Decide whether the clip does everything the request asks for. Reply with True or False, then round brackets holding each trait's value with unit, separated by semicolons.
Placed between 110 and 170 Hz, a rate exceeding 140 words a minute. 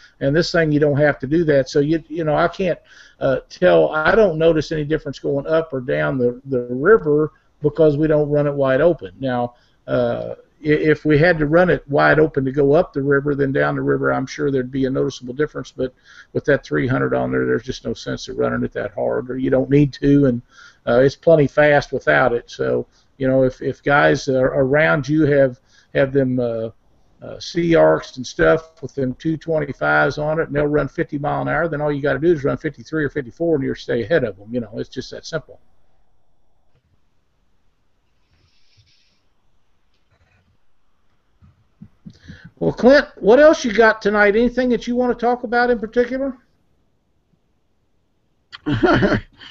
True (140 Hz; 200 wpm)